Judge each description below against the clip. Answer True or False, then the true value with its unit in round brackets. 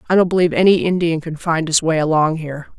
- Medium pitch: True (165 Hz)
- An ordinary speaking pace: False (235 wpm)